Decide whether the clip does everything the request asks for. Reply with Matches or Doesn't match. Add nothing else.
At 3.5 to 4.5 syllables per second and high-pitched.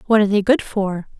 Doesn't match